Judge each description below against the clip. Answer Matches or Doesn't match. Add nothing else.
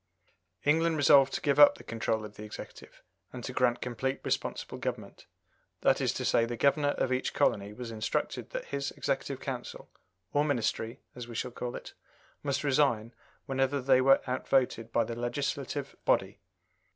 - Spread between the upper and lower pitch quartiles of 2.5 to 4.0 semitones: Matches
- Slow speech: Doesn't match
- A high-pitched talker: Doesn't match